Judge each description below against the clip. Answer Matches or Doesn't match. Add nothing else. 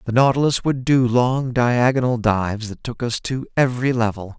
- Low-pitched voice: Matches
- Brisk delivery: Doesn't match